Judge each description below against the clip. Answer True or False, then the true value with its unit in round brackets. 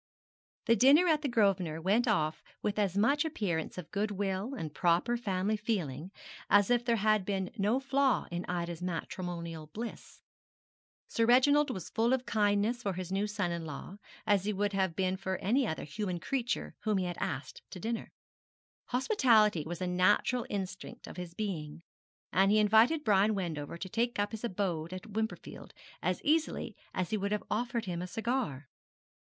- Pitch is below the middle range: False (205 Hz)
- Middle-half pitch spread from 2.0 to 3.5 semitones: False (4.4 semitones)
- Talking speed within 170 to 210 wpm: True (175 wpm)